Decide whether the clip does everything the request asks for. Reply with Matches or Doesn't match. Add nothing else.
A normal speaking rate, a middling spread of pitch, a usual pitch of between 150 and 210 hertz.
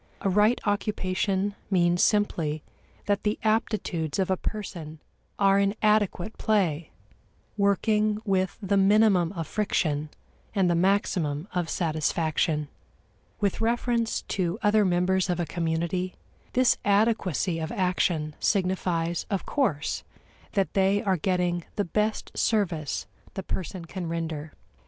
Doesn't match